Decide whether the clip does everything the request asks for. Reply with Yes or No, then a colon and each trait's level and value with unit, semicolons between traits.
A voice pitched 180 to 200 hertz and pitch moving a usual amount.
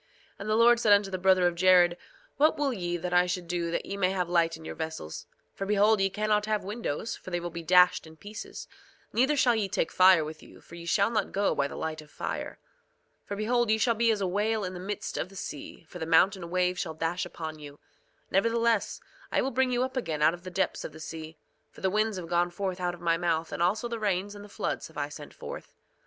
Yes: medium, 185 Hz; average, 3.9 semitones